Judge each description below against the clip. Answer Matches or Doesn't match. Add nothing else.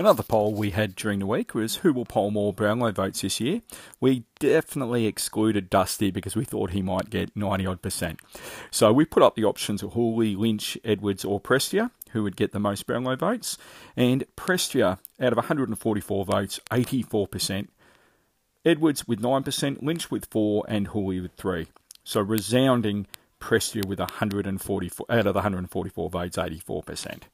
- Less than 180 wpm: Matches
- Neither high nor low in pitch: Doesn't match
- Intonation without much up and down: Doesn't match